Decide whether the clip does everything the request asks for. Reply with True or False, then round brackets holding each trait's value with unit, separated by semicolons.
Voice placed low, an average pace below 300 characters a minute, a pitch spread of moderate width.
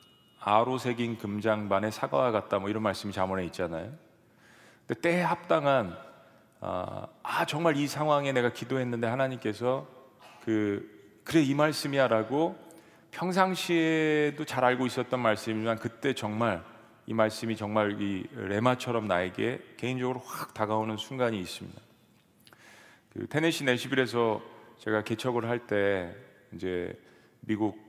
True (120 Hz; 290 characters per minute; 3.9 semitones)